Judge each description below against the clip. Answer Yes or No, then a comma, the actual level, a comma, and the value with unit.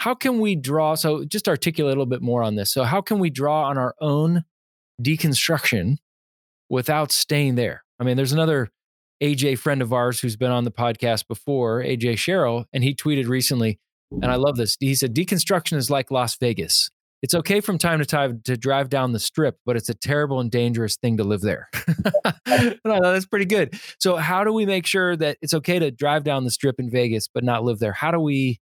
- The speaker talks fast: Yes, fast, 220 wpm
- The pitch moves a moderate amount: Yes, average, 4.7 semitones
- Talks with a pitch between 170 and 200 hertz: No, medium, 140 Hz